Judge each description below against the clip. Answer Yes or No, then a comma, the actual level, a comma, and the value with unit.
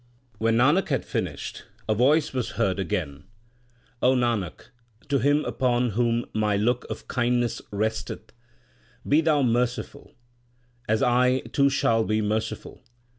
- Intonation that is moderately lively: Yes, average, 3.1 semitones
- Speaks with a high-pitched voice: No, low, 120 Hz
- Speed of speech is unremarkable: No, slow, 130 wpm